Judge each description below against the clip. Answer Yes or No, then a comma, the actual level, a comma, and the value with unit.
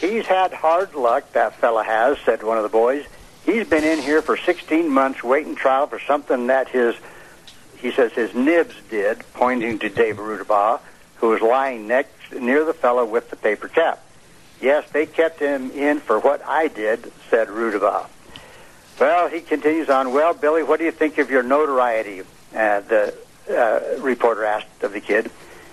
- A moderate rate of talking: Yes, average, 180 wpm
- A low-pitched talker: No, medium, 155 Hz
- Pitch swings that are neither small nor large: No, wide, 7.7 semitones